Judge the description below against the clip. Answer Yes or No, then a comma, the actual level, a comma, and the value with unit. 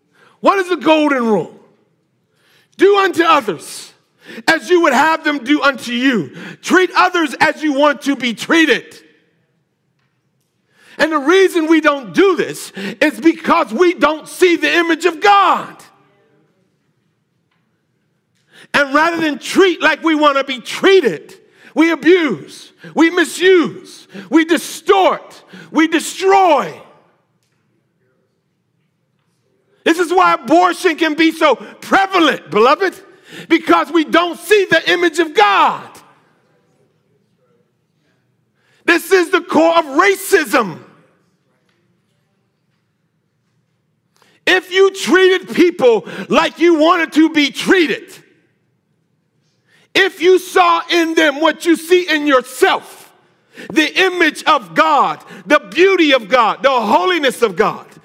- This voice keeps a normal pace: No, slow, 115 wpm